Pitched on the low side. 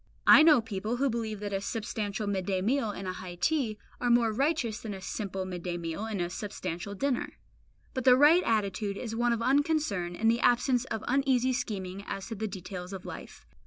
No: high, 215 Hz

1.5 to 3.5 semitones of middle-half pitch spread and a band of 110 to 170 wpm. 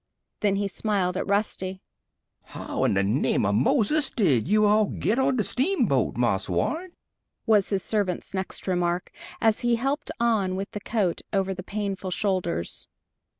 Yes: average, 3.0 semitones; average, 160 wpm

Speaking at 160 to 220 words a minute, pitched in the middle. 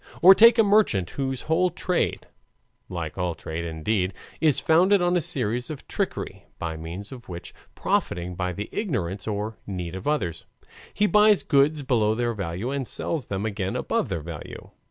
No: average, 175 wpm; low, 110 Hz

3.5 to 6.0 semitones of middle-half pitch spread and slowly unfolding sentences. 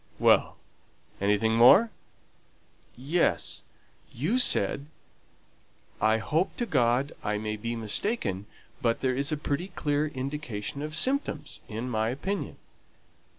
Yes: wide, 5.5 semitones; slow, 120 wpm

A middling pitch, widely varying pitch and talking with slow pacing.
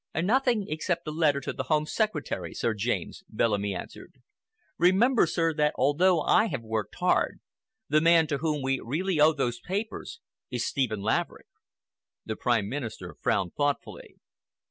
No: medium, 150 Hz; wide, 6.6 semitones; average, 150 wpm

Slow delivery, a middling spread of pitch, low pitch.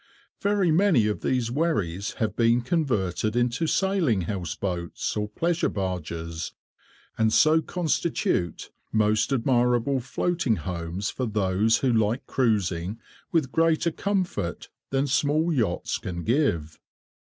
No: slow, 120 wpm; wide, 8.3 semitones; low, 115 Hz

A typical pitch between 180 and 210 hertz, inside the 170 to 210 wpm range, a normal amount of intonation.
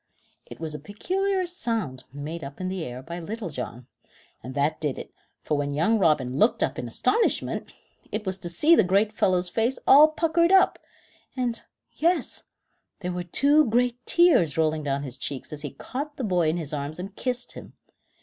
No: medium, 185 Hz; average, 190 wpm; wide, 8.8 semitones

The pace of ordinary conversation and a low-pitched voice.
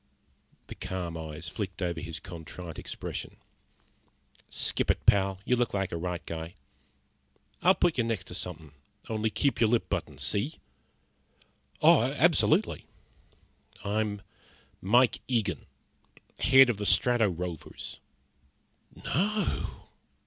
No: slow, 120 wpm; low, 100 Hz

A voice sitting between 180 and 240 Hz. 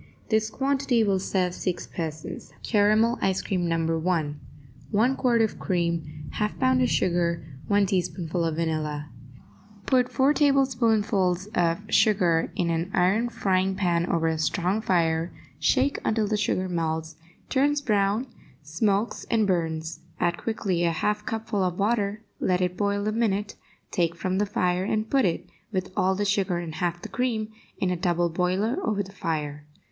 Yes: high, 190 Hz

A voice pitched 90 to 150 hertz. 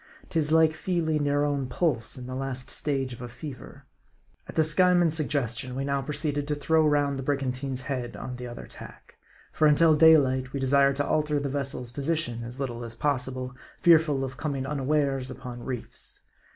Yes: medium, 140 Hz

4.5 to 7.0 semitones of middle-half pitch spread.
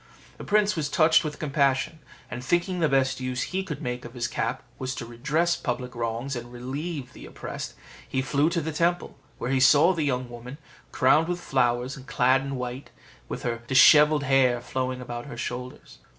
No: average, 3.7 semitones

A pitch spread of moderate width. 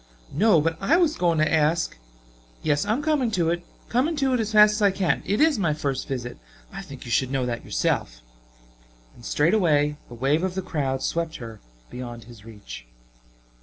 No: wide, 8.5 semitones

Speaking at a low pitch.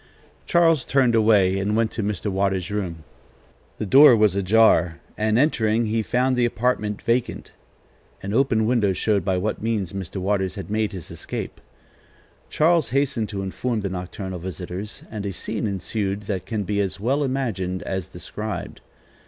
Yes: low, 105 Hz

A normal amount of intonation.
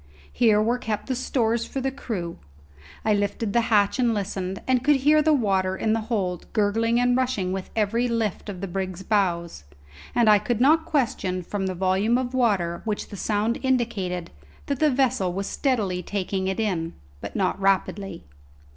Yes: average, 4.3 semitones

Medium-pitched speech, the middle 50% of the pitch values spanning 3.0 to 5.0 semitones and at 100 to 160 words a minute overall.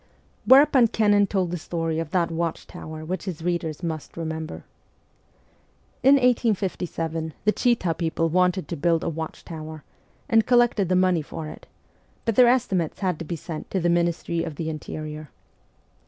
Yes: medium, 170 Hz; average, 3.6 semitones; average, 155 wpm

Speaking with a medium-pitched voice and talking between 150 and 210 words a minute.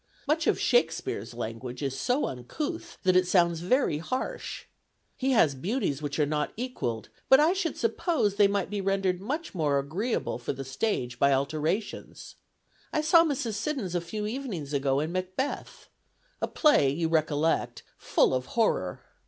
Yes: medium, 180 Hz; average, 160 wpm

